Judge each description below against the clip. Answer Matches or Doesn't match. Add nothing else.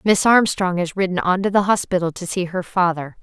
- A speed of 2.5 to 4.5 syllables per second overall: Doesn't match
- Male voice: Doesn't match